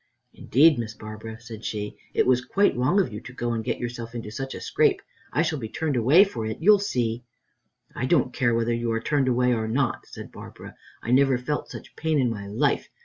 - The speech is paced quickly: Yes, fast, 225 wpm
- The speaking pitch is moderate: No, low, 120 Hz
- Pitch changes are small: No, average, 3.4 semitones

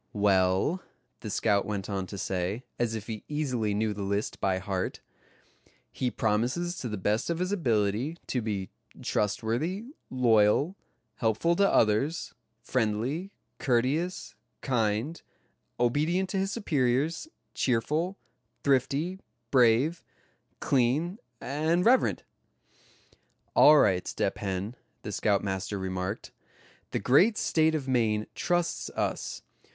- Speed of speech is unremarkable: No, slow, 115 wpm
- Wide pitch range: Yes, wide, 7.4 semitones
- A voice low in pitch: Yes, low, 120 Hz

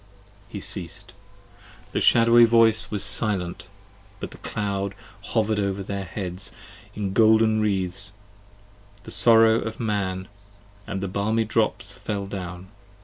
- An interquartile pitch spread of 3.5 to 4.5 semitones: No, narrow, 2.4 semitones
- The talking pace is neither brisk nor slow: No, slow, 125 wpm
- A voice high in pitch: No, low, 100 Hz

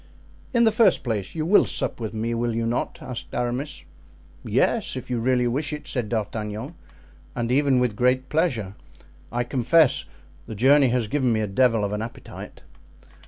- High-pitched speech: No, low, 120 Hz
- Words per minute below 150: No, average, 175 wpm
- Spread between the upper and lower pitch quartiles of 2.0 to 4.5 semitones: Yes, average, 3.3 semitones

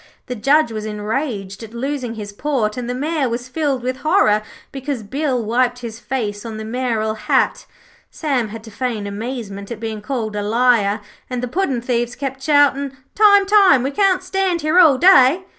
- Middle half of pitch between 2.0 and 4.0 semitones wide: No, average, 4.6 semitones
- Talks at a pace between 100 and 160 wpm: No, average, 185 wpm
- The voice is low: No, very high, 250 Hz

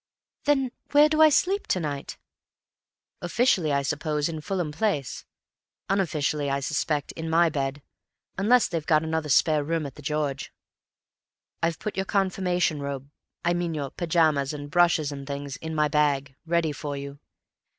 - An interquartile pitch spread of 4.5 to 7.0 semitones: No, average, 3.5 semitones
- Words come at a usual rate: Yes, average, 150 wpm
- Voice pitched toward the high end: No, medium, 155 Hz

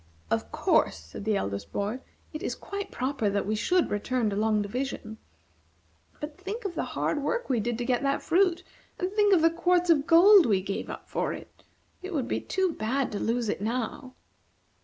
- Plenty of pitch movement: Yes, wide, 8.4 semitones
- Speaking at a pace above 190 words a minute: Yes, average, 200 wpm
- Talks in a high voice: Yes, very high, 260 Hz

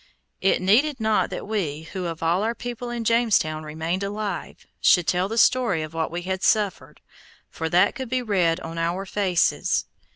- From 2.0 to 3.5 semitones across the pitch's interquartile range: No, average, 4.9 semitones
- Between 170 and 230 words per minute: Yes, average, 185 wpm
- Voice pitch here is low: No, high, 190 Hz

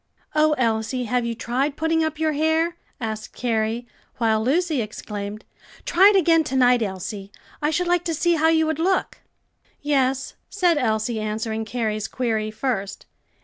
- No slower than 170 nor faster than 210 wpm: No, average, 160 wpm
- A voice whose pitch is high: Yes, very high, 250 Hz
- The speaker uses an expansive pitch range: Yes, wide, 6.5 semitones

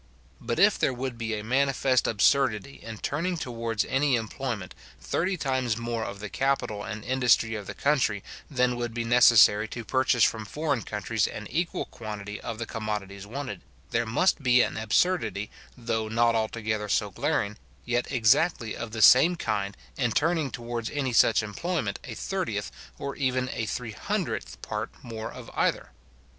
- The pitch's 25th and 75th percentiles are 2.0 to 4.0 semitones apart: Yes, average, 3.4 semitones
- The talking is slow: No, average, 165 wpm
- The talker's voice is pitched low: Yes, low, 115 Hz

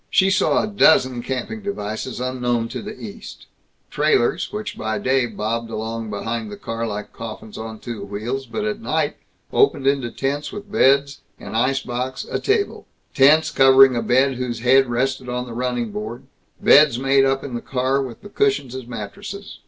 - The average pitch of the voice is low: Yes, low, 130 Hz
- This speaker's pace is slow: No, average, 180 wpm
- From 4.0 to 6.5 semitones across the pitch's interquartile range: No, average, 3.2 semitones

